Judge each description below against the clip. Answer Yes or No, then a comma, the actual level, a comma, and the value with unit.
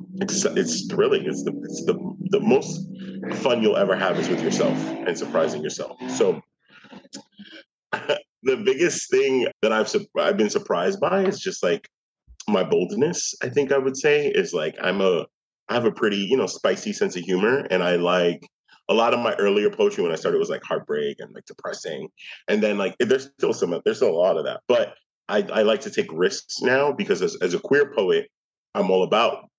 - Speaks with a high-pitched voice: Yes, high, 210 Hz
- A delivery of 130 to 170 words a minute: No, fast, 205 wpm